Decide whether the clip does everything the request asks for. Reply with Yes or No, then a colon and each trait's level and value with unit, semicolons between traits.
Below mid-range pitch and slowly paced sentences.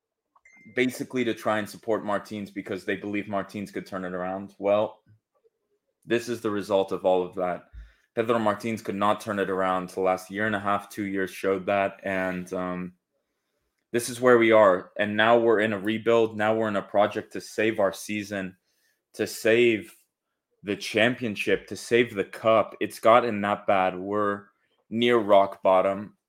No: low, 105 Hz; average, 180 wpm